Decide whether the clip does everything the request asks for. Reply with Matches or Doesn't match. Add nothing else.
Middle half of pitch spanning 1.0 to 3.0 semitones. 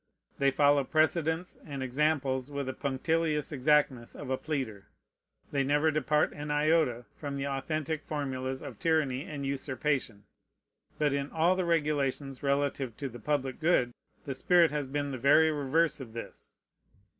Matches